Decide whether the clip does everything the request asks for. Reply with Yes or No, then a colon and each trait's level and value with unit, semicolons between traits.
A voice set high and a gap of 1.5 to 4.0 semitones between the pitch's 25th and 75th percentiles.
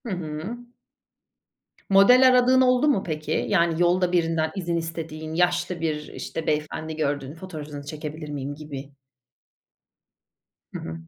No: medium, 160 Hz; average, 3.0 semitones